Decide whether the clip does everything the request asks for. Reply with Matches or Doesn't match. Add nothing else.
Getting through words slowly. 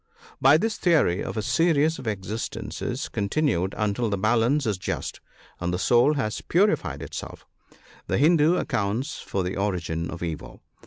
Doesn't match